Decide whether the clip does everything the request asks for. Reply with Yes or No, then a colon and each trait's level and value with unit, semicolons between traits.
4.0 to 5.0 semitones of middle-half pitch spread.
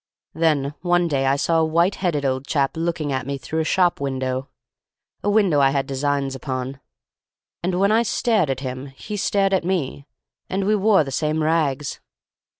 Yes: average, 4.7 semitones